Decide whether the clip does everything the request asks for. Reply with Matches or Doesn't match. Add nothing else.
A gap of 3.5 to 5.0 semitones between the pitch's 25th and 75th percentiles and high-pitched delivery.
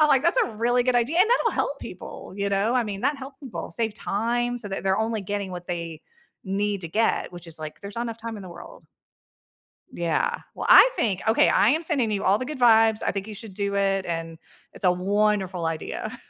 Matches